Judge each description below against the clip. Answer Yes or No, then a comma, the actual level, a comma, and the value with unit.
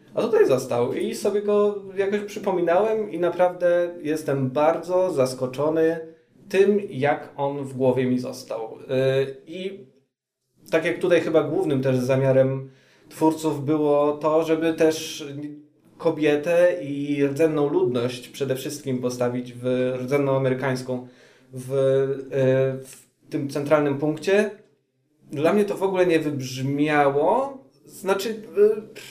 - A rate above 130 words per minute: No, average, 120 wpm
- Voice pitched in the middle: Yes, medium, 150 Hz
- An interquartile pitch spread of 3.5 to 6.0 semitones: Yes, average, 4.4 semitones